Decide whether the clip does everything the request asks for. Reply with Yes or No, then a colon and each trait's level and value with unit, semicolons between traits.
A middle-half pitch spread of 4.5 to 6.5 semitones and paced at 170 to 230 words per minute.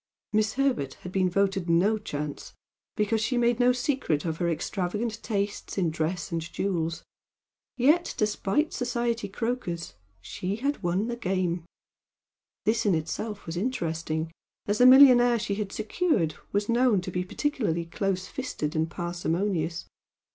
No: wide, 5.6 semitones; average, 145 wpm